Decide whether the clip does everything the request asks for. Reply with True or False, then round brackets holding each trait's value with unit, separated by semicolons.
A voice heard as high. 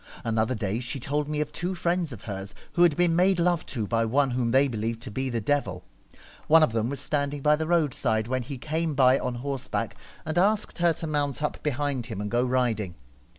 False (135 Hz)